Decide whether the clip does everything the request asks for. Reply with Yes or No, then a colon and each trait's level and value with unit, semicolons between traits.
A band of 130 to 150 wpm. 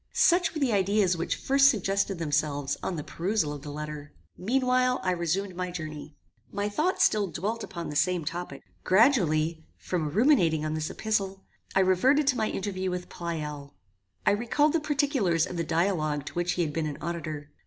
No: average, 185 wpm